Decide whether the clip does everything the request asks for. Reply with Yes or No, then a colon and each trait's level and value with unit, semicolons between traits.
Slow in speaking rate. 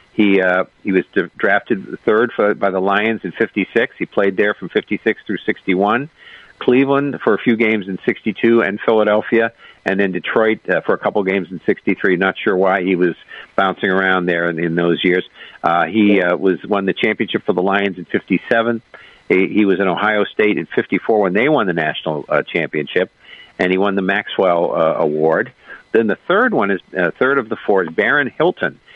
No: average, 200 wpm